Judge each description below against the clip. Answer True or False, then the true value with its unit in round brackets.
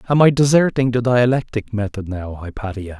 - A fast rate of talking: False (160 wpm)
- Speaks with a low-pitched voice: True (115 Hz)